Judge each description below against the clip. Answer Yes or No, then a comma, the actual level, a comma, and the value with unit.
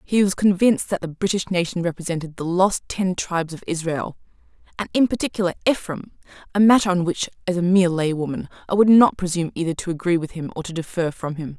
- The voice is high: No, medium, 175 Hz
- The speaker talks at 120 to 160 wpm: No, average, 200 wpm